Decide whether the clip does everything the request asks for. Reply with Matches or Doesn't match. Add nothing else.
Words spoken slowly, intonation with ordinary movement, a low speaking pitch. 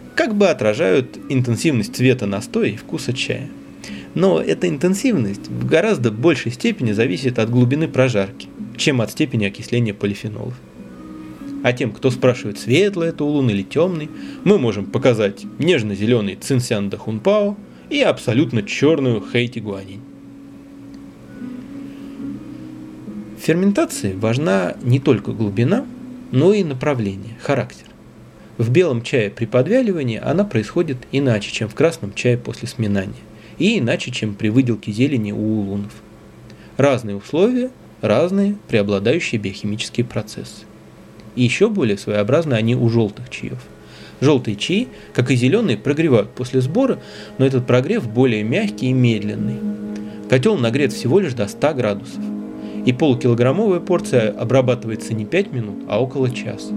Doesn't match